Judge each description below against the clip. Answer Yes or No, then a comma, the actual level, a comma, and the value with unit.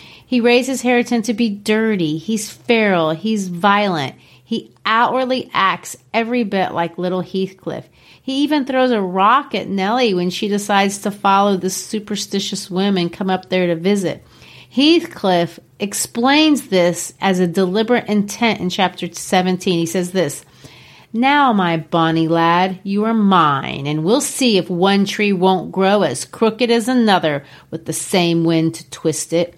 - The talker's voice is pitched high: Yes, high, 195 Hz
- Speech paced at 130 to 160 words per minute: Yes, average, 155 wpm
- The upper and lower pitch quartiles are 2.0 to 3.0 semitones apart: No, average, 4.3 semitones